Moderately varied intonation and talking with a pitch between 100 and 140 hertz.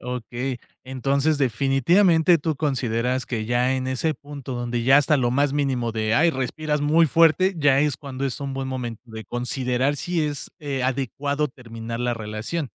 Yes: average, 3.2 semitones; low, 135 Hz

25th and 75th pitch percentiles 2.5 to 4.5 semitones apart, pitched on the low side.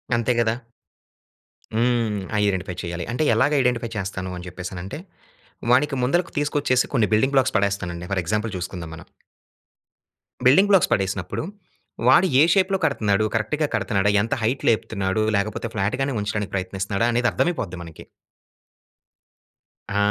No: average, 5.0 semitones; low, 110 Hz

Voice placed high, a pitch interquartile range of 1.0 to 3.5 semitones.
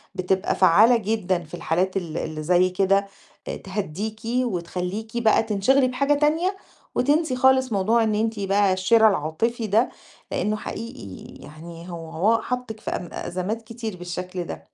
No: high, 200 Hz; average, 4.3 semitones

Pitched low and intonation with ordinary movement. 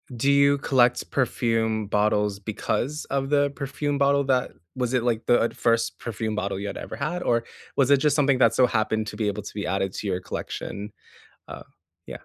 Yes: low, 115 Hz; average, 4.7 semitones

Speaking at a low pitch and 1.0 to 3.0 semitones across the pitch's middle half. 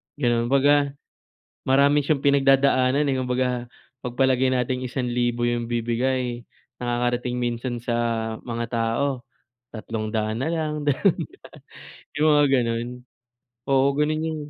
Yes: low, 125 Hz; average, 2.7 semitones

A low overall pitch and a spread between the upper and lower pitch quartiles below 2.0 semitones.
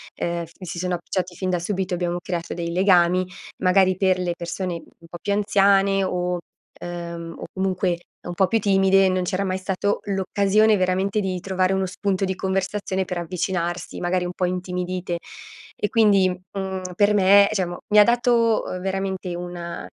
No: medium, 185 Hz; narrow, 1.5 semitones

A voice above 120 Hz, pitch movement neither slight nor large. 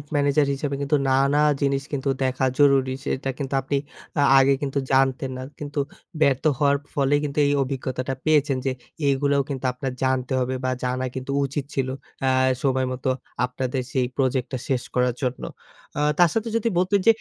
No: low, 135 Hz; narrow, 1.6 semitones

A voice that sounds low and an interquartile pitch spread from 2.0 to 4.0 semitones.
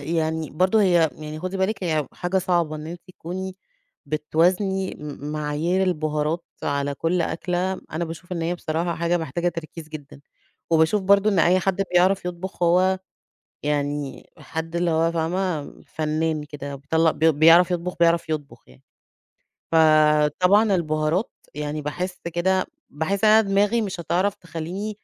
No: medium, 170 Hz; average, 3.1 semitones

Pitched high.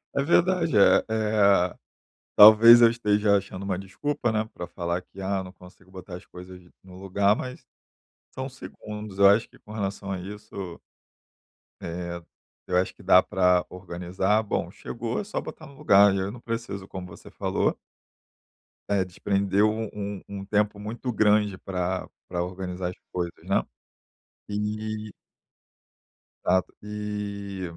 No: low, 100 Hz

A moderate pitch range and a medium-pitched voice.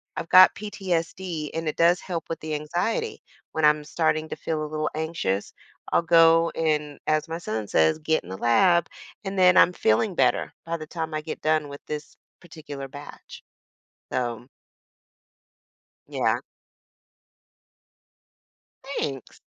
No: narrow, 2.3 semitones; medium, 160 Hz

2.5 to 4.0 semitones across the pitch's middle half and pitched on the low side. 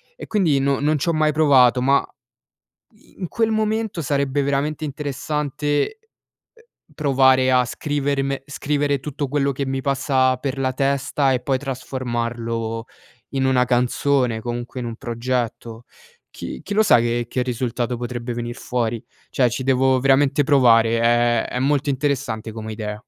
Yes: average, 2.9 semitones; low, 130 Hz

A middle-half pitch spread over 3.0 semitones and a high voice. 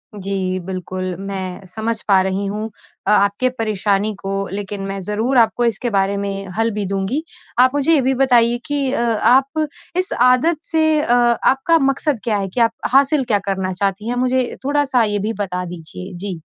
Yes: average, 4.7 semitones; high, 220 Hz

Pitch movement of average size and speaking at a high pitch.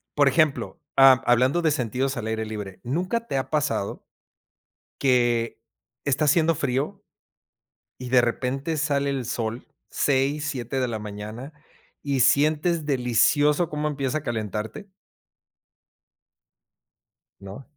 No: average, 3.9 semitones; low, 135 Hz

